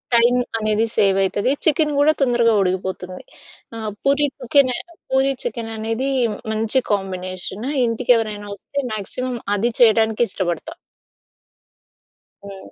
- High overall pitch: Yes, high, 225 Hz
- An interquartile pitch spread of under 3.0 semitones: No, average, 4.0 semitones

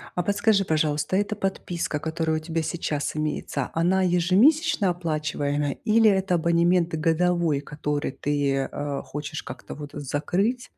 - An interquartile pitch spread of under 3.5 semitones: No, average, 3.8 semitones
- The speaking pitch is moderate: Yes, medium, 165 Hz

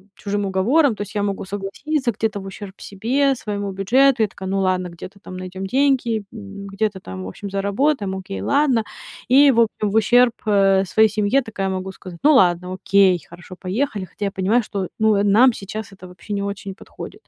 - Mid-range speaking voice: No, high, 200 Hz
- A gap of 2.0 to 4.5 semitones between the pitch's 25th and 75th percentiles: Yes, average, 2.9 semitones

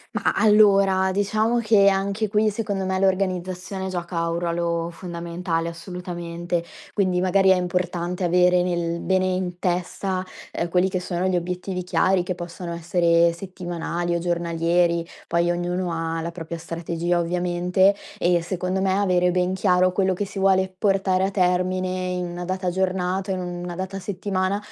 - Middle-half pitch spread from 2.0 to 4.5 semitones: No, narrow, 1.6 semitones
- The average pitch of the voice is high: No, medium, 180 Hz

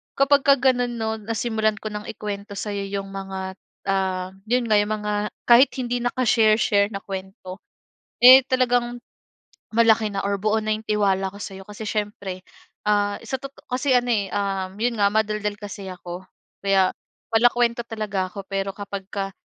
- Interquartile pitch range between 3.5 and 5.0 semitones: No, average, 3.1 semitones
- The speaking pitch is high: Yes, high, 210 Hz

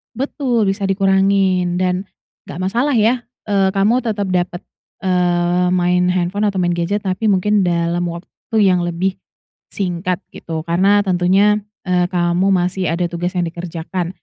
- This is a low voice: No, medium, 185 Hz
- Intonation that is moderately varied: No, narrow, 2.1 semitones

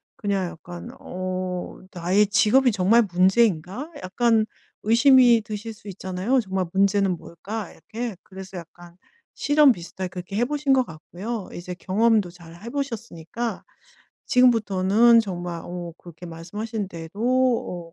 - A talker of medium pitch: No, high, 200 Hz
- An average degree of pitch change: Yes, average, 4.6 semitones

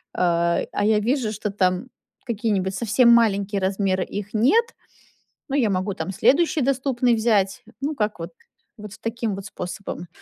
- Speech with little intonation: No, average, 3.7 semitones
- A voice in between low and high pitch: No, high, 210 Hz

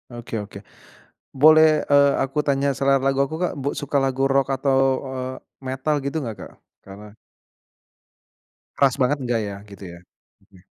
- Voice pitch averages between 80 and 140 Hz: Yes, low, 135 Hz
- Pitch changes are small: Yes, narrow, 2.3 semitones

